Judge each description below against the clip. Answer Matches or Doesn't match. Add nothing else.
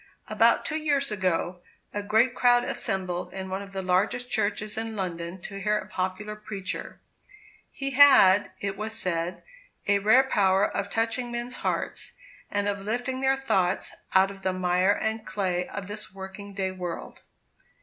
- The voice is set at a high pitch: Matches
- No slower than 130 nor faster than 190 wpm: Matches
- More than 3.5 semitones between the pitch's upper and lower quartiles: Doesn't match